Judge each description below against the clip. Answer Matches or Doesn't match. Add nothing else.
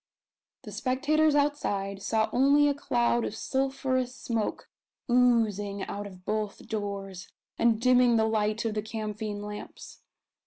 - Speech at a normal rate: Doesn't match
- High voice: Matches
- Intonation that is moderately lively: Matches